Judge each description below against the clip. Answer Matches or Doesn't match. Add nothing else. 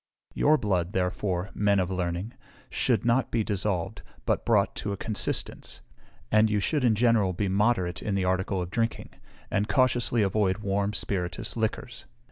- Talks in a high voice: Doesn't match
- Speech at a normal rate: Matches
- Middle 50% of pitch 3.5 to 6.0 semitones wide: Doesn't match